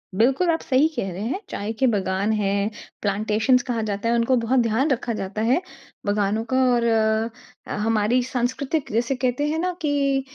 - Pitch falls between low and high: No, high, 235 Hz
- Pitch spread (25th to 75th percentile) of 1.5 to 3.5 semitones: No, average, 3.9 semitones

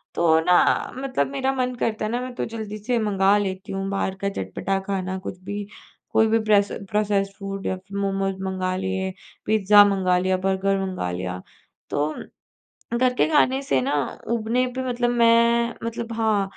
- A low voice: No, high, 200 Hz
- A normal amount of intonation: Yes, average, 3.4 semitones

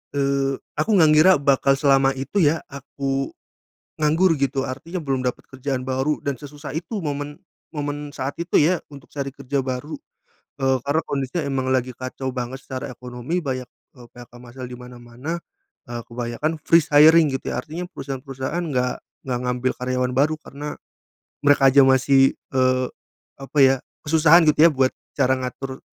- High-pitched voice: No, low, 135 Hz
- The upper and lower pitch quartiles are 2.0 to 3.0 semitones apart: Yes, narrow, 2.5 semitones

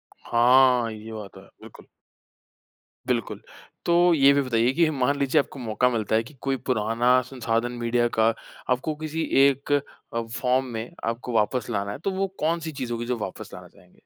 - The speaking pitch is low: Yes, low, 125 Hz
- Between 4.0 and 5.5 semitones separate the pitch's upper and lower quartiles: No, average, 3.3 semitones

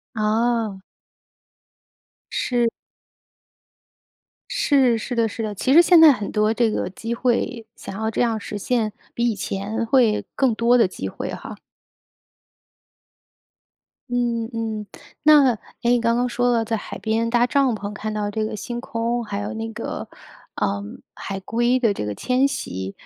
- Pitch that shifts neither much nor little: No, narrow, 2.3 semitones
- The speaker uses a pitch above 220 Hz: Yes, high, 230 Hz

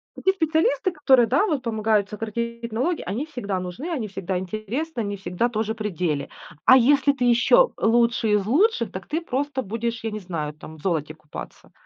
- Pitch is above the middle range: Yes, high, 230 Hz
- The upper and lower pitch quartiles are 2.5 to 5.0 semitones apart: No, wide, 5.6 semitones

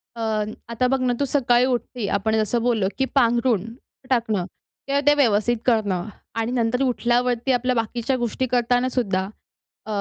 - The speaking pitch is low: No, high, 240 Hz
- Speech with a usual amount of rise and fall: No, narrow, 2.1 semitones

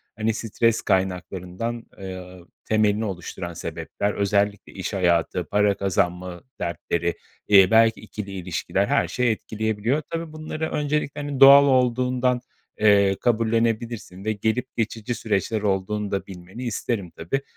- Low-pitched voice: Yes, low, 105 Hz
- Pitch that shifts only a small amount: No, average, 3.9 semitones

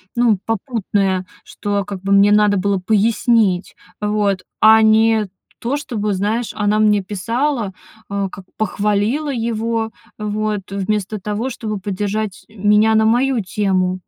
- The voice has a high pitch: Yes, high, 210 Hz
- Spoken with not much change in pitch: Yes, narrow, 1.9 semitones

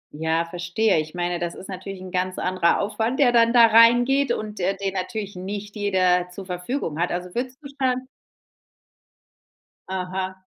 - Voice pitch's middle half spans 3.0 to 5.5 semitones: Yes, average, 4.2 semitones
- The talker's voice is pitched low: No, high, 190 Hz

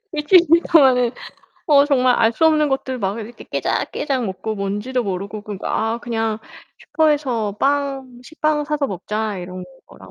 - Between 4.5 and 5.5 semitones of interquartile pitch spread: Yes, average, 5.2 semitones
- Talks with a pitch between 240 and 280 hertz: Yes, high, 245 Hz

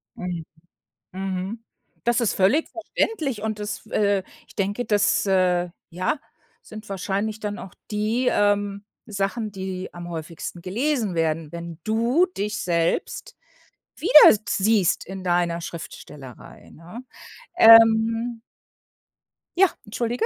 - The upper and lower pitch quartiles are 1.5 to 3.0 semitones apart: No, average, 3.8 semitones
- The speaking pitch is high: Yes, high, 205 Hz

